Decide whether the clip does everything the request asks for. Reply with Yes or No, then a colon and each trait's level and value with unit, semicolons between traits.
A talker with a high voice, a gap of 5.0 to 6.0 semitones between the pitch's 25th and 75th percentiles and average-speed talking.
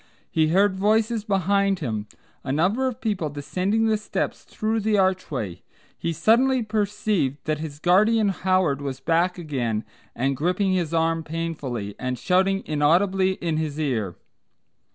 No: medium, 175 Hz; wide, 5.5 semitones; average, 145 wpm